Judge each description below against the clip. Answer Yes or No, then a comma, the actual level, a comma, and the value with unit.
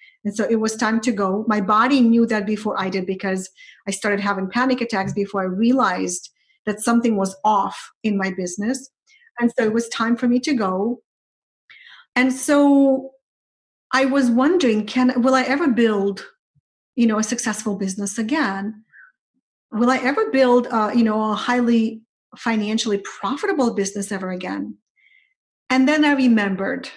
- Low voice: No, high, 230 Hz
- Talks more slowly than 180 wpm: Yes, average, 160 wpm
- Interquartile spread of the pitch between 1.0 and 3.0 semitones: No, average, 3.8 semitones